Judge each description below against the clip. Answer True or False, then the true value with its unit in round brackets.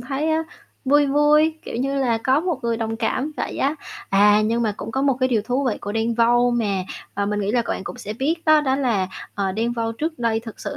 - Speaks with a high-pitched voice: True (240 Hz)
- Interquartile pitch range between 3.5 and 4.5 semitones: True (3.9 semitones)